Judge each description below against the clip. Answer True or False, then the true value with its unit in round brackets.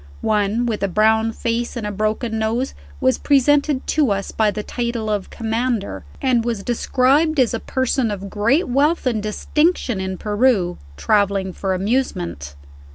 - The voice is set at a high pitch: True (225 Hz)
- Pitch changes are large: False (3.9 semitones)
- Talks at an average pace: True (160 wpm)